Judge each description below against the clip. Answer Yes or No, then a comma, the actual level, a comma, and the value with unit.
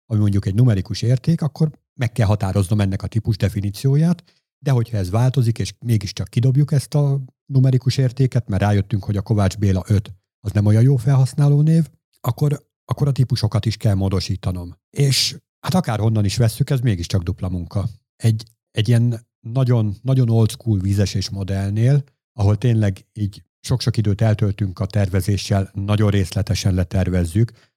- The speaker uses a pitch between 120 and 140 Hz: No, low, 110 Hz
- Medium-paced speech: No, fast, 160 wpm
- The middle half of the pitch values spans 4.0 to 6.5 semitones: Yes, average, 4.4 semitones